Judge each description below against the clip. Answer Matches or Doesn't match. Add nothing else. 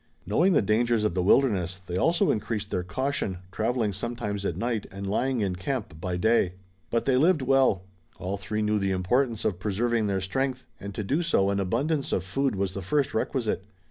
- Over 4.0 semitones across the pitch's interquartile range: Matches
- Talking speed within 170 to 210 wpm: Matches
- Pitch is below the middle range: Matches